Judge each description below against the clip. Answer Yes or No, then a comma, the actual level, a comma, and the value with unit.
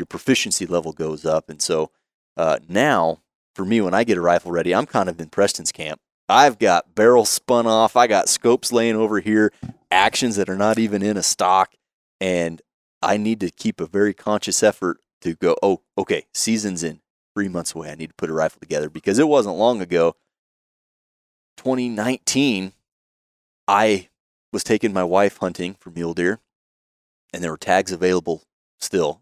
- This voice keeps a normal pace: Yes, average, 180 wpm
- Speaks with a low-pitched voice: Yes, very low, 95 Hz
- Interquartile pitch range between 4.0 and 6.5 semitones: Yes, average, 4.5 semitones